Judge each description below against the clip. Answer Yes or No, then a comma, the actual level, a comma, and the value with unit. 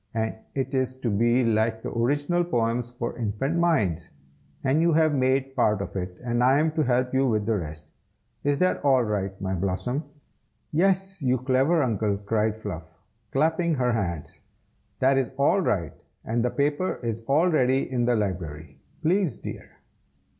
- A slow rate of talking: No, average, 170 wpm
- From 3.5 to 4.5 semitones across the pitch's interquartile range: No, average, 5.0 semitones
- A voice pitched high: No, low, 125 Hz